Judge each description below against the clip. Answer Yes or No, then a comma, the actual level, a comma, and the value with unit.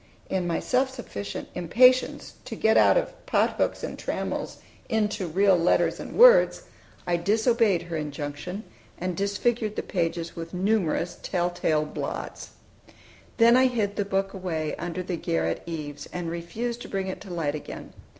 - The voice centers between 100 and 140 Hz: No, medium, 185 Hz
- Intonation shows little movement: No, average, 4.7 semitones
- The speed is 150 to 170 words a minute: Yes, average, 160 wpm